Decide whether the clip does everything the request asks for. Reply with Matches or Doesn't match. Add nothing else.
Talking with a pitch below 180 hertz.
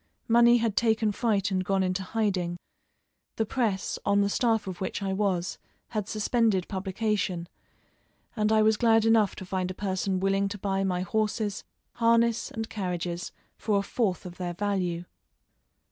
Doesn't match